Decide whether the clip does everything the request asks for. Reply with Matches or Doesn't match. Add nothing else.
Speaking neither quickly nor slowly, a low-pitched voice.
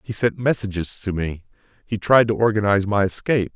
Matches